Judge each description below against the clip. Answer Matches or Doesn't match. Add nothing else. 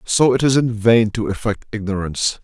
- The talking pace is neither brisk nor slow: Matches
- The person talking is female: Doesn't match